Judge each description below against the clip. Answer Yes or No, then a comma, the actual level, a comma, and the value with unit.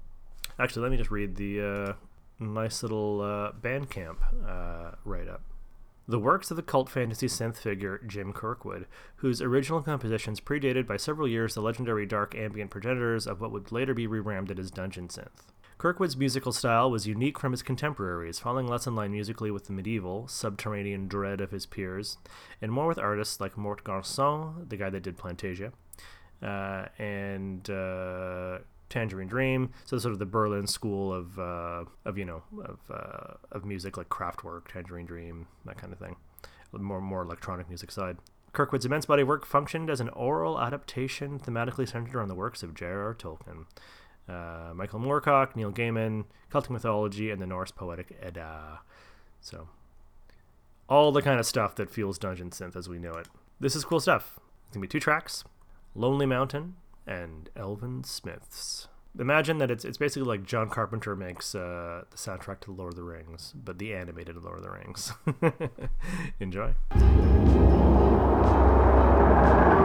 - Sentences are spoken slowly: No, average, 165 wpm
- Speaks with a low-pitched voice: Yes, low, 100 Hz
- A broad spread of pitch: No, average, 4.9 semitones